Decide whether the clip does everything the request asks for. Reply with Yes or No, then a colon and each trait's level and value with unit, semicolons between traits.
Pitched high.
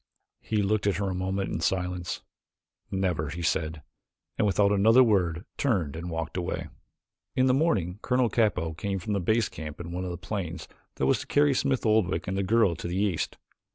No: very low, 95 Hz